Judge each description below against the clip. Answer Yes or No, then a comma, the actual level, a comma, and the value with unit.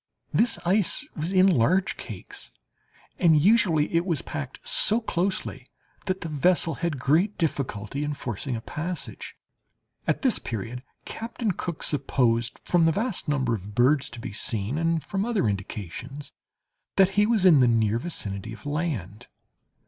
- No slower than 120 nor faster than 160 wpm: Yes, average, 155 wpm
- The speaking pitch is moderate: Yes, medium, 150 Hz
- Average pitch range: No, wide, 7.6 semitones